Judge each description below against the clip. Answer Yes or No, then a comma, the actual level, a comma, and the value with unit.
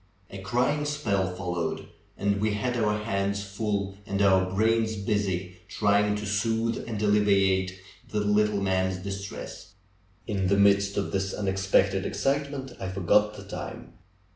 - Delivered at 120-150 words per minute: Yes, average, 140 wpm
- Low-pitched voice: Yes, low, 100 Hz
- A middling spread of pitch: No, narrow, 1.6 semitones